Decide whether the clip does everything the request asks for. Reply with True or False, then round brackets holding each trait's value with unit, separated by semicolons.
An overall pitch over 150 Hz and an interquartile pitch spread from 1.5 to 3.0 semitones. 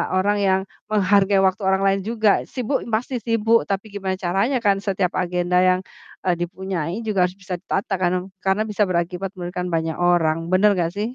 True (190 Hz; 2.4 semitones)